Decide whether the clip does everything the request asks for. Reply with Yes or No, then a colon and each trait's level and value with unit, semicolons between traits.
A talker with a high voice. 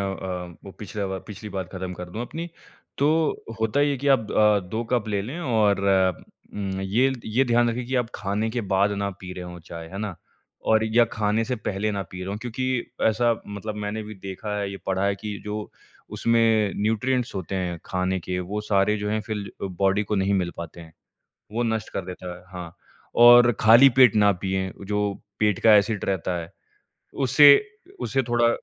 No: low, 105 Hz